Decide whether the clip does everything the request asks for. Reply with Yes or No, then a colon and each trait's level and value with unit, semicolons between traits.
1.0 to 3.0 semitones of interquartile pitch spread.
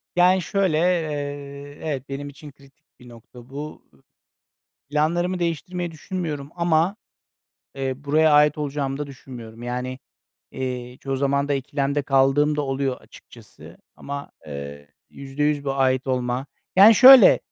Yes: average, 2.7 semitones